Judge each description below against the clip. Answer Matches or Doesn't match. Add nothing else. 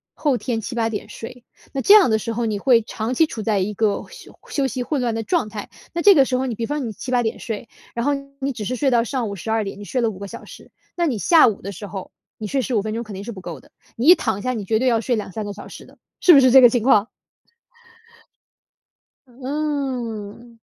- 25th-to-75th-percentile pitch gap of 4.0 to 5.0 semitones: Doesn't match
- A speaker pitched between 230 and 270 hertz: Matches